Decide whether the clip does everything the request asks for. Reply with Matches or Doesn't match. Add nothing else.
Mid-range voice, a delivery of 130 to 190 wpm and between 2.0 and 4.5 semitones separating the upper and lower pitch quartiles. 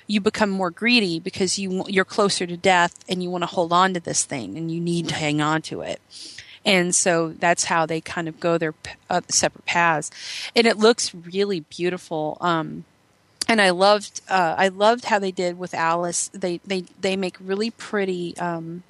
Doesn't match